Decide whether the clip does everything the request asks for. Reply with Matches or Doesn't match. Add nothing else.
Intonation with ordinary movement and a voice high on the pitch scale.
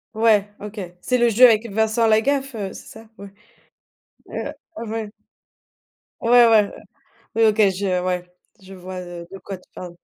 Matches